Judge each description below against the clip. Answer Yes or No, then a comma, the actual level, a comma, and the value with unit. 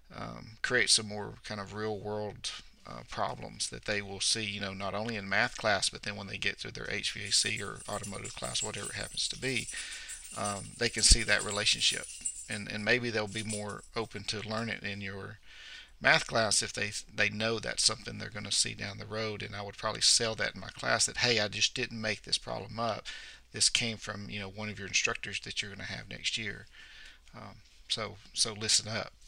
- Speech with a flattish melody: Yes, narrow, 1.4 semitones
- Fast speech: Yes, fast, 220 wpm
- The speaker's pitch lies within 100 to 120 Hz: Yes, low, 105 Hz